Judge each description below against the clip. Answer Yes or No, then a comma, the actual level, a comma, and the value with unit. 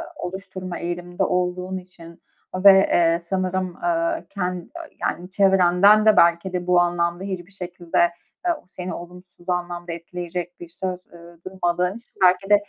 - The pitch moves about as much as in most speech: No, narrow, 1.3 semitones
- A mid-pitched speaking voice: Yes, medium, 180 Hz